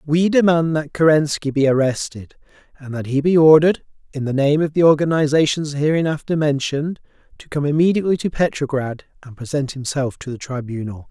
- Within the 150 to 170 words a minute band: Yes, average, 160 wpm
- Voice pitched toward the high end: No, medium, 145 Hz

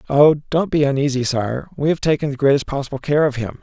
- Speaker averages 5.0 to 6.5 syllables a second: Yes, 6.0 syllables/s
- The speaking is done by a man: Yes, male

